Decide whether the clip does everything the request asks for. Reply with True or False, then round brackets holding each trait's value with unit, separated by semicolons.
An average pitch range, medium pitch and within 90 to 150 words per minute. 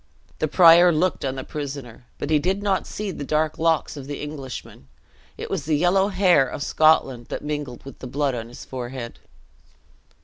False (4.0 semitones; 150 Hz; 190 wpm)